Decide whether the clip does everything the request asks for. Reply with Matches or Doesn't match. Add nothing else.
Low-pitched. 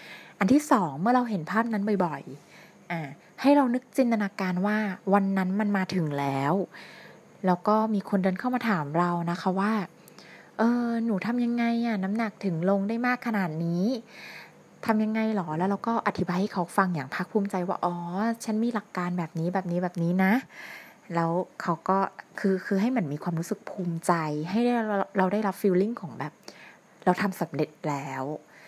Doesn't match